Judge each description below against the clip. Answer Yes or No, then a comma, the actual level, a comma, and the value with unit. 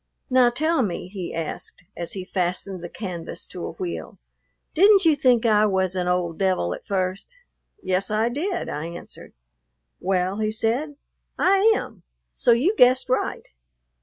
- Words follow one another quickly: No, average, 160 wpm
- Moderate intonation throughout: No, wide, 6.1 semitones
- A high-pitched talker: Yes, high, 210 Hz